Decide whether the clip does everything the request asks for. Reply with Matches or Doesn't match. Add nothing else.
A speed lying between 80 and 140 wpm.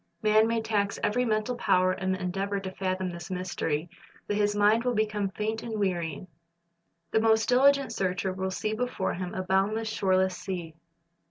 Doesn't match